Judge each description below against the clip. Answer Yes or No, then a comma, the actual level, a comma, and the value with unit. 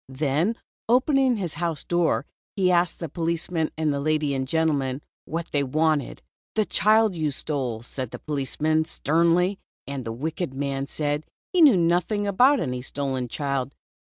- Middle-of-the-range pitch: Yes, medium, 155 Hz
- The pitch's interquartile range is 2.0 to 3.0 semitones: No, average, 4.1 semitones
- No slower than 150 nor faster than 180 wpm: Yes, average, 160 wpm